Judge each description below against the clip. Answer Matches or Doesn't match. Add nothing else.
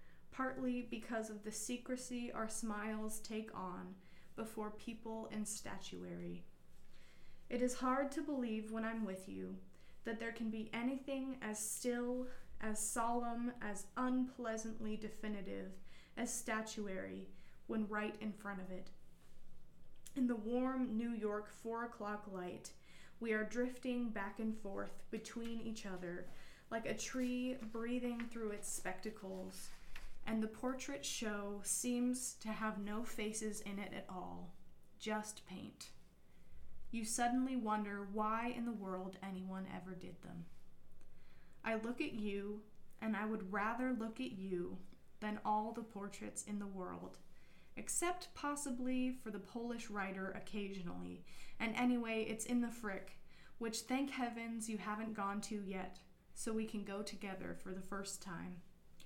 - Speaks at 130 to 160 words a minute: Matches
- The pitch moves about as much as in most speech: Matches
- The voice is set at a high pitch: Matches